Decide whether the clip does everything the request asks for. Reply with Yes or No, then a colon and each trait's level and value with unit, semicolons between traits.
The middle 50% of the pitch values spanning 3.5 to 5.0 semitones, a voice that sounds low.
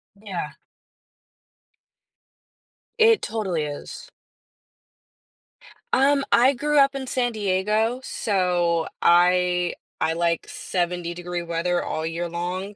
No: average, 4.7 semitones; medium, 180 Hz